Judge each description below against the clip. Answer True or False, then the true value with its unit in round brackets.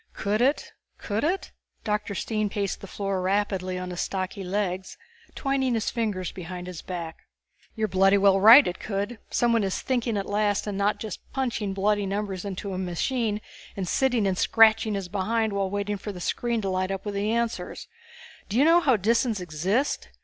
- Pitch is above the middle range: True (205 Hz)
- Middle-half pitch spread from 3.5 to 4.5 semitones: False (2.9 semitones)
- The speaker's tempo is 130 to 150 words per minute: False (190 wpm)